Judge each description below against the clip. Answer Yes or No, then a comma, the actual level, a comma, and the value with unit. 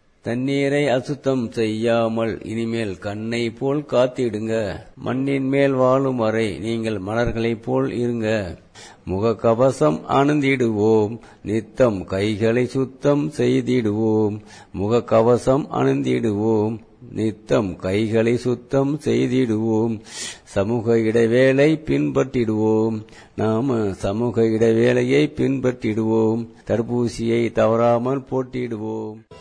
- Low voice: Yes, low, 115 Hz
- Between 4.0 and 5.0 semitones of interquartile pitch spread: No, average, 2.7 semitones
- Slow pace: Yes, slow, 75 wpm